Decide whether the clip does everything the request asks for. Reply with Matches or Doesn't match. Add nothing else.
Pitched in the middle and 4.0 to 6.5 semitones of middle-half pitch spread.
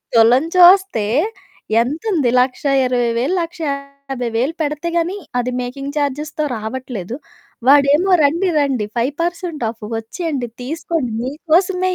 Doesn't match